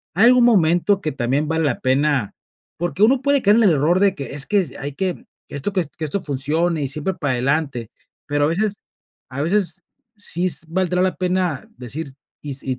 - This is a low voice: No, medium, 160 Hz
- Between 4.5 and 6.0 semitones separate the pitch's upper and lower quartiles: Yes, average, 5.1 semitones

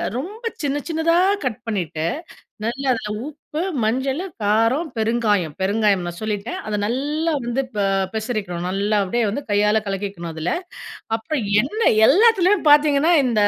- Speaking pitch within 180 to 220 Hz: No, high, 230 Hz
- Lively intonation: Yes, wide, 6.2 semitones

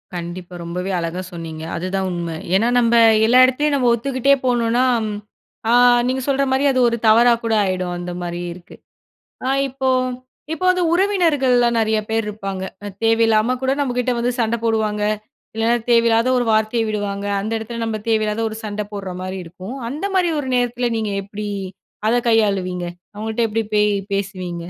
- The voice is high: Yes, high, 220 Hz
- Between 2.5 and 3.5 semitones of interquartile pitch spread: No, average, 4.0 semitones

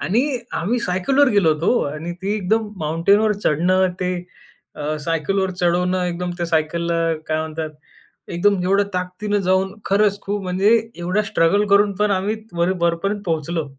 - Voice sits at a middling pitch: Yes, medium, 180 Hz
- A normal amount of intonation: Yes, average, 3.1 semitones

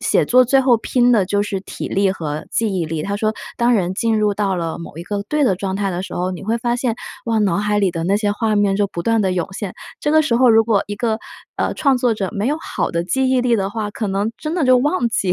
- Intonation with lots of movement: No, average, 3.7 semitones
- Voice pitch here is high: Yes, high, 210 Hz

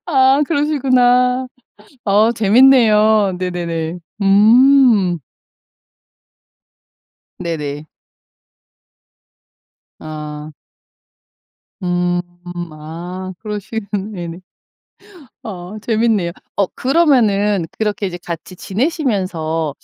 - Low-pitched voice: No, high, 200 Hz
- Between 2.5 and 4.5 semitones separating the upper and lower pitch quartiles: No, wide, 5.4 semitones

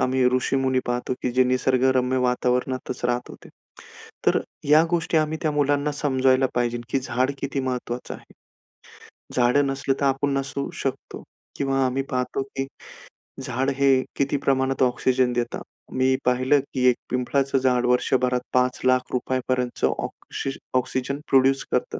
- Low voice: Yes, low, 130 Hz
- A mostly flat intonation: Yes, narrow, 1.3 semitones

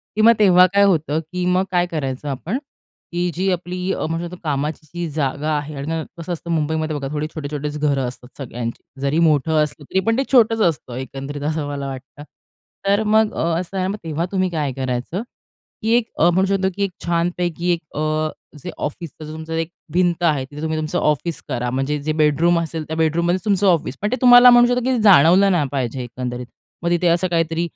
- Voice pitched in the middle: Yes, medium, 160 Hz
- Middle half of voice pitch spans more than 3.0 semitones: Yes, average, 3.6 semitones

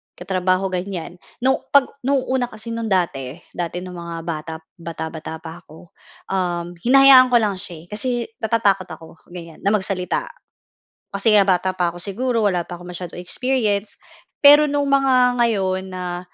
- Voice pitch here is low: No, high, 190 Hz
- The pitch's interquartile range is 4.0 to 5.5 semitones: Yes, average, 5.1 semitones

